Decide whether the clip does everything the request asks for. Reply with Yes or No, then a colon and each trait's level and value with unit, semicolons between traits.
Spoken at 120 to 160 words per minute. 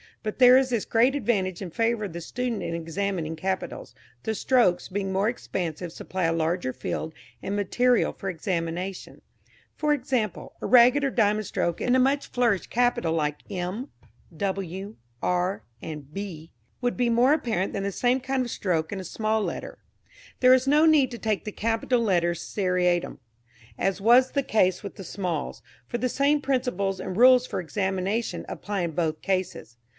No: average, 175 wpm